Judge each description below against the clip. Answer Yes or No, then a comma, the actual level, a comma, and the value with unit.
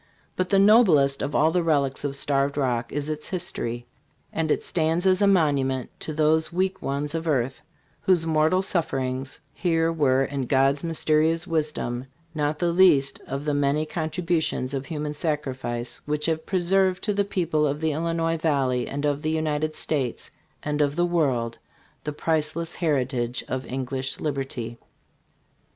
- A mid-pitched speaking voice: Yes, medium, 150 Hz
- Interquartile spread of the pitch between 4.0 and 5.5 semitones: No, average, 3.3 semitones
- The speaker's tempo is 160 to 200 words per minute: Yes, average, 165 wpm